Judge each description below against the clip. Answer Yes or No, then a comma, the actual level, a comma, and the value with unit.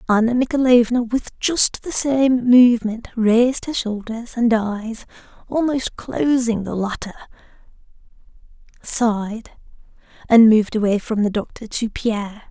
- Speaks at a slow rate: Yes, slow, 120 wpm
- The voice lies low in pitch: No, high, 230 Hz